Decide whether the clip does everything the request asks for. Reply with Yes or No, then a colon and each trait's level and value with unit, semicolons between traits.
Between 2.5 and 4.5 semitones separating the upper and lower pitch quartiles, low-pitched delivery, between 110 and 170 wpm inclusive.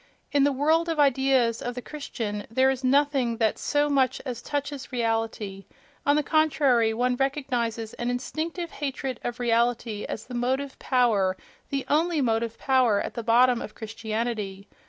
No: average, 3.6 semitones; very high, 250 Hz; average, 160 wpm